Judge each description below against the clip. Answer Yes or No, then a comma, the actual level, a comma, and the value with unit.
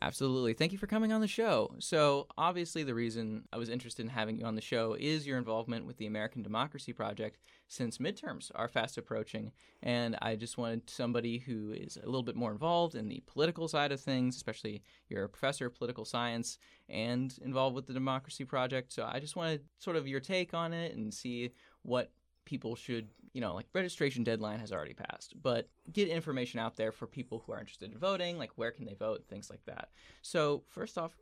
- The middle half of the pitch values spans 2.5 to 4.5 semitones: No, average, 4.9 semitones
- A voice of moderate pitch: No, low, 125 Hz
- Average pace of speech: No, fast, 215 wpm